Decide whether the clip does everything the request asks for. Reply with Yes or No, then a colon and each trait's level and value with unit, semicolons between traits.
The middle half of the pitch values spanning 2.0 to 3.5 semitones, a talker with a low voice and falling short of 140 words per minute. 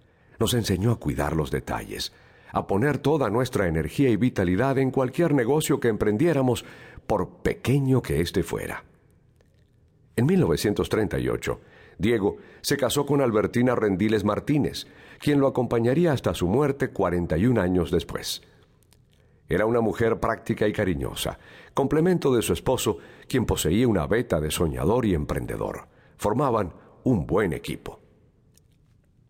No: average, 5.3 semitones; low, 120 Hz; average, 130 wpm